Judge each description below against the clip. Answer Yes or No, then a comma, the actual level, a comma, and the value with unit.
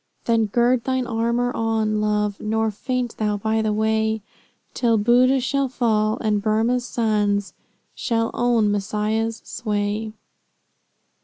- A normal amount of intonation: No, narrow, 2.0 semitones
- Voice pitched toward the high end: Yes, high, 220 Hz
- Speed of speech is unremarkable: No, slow, 125 wpm